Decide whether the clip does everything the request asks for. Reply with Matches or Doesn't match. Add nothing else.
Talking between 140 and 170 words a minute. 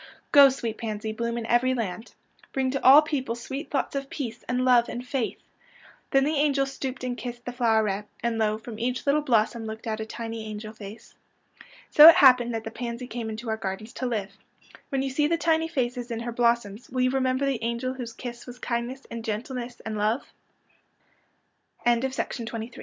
Doesn't match